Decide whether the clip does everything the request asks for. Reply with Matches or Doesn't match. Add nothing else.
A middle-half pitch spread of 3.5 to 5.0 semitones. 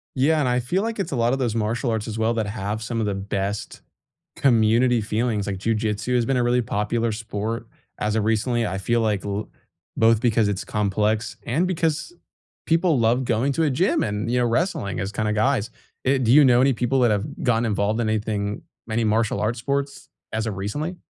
Doesn't match